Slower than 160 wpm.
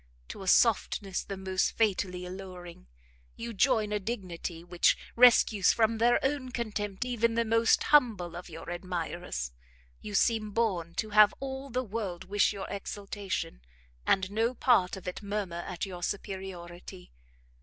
Yes: average, 150 wpm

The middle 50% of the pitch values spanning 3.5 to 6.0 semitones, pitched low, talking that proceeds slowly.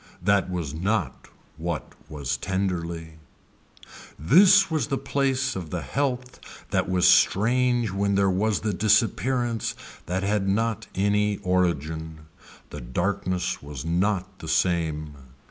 Yes: average, 4.9 semitones; very low, 95 Hz; slow, 125 wpm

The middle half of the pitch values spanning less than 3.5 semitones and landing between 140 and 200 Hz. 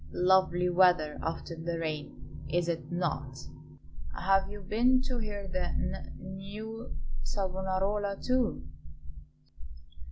Yes: average, 3.0 semitones; high, 190 Hz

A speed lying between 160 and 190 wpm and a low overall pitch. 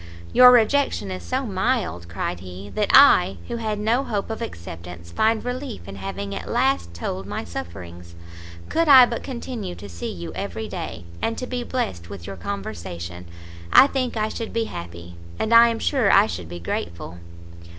Yes: average, 180 wpm; low, 100 Hz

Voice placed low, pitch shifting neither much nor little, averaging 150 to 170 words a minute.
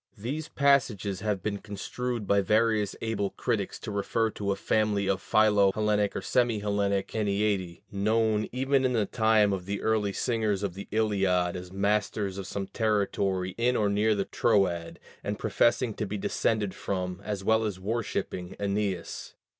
No: low, 105 Hz; narrow, 2.1 semitones; average, 165 wpm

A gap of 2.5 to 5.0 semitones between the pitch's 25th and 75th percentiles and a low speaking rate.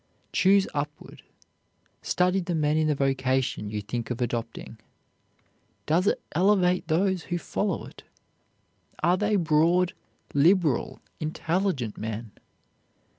No: wide, 5.5 semitones; slow, 115 wpm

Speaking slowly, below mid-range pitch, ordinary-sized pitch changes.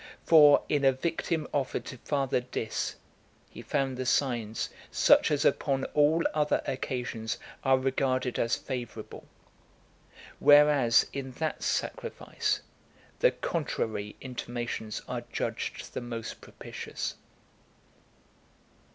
Yes: slow, 110 wpm; low, 130 Hz; average, 3.4 semitones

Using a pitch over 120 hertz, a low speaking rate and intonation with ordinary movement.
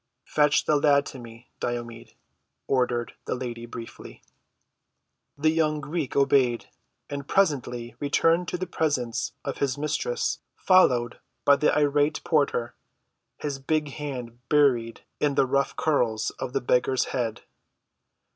Yes: medium, 140 Hz; slow, 130 wpm; average, 3.6 semitones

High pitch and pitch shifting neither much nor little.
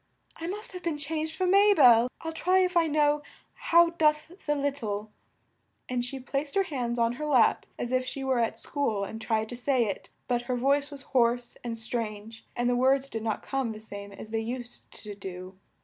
Yes: very high, 255 Hz; average, 4.8 semitones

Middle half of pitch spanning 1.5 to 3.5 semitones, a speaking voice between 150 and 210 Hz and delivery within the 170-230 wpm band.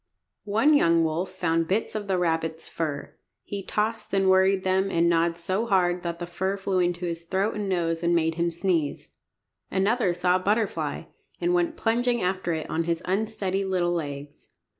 Yes: average, 2.9 semitones; medium, 185 Hz; average, 185 wpm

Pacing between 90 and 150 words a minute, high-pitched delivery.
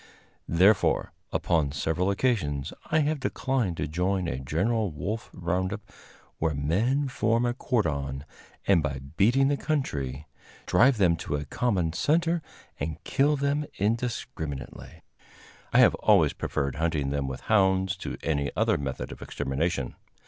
No: average, 140 wpm; very low, 90 Hz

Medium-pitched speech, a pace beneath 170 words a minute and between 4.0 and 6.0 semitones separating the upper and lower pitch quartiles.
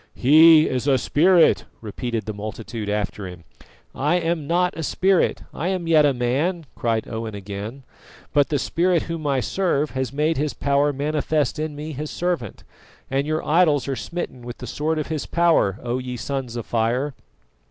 No: medium, 145 Hz; average, 180 wpm; average, 4.9 semitones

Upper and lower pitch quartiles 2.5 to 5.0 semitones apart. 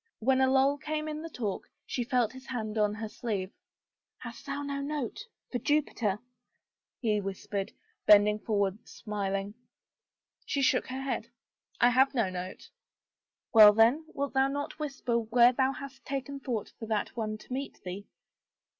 Yes: average, 4.5 semitones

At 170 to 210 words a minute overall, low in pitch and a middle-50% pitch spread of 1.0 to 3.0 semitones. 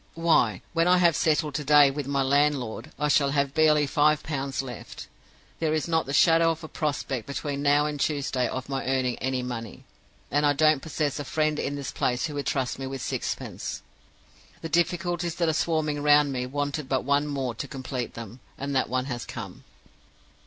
No: average, 200 wpm; medium, 145 Hz; narrow, 2.4 semitones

